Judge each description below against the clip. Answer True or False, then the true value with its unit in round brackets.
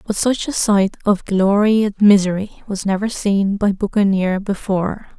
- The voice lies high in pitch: True (200 Hz)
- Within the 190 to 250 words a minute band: False (160 wpm)